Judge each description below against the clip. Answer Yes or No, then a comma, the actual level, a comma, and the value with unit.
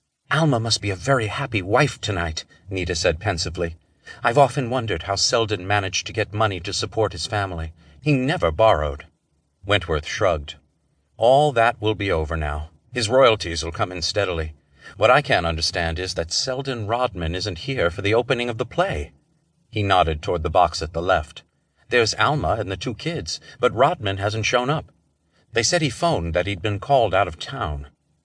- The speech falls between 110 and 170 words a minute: No, average, 185 wpm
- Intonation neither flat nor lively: No, wide, 6.1 semitones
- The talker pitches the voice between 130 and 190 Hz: No, low, 100 Hz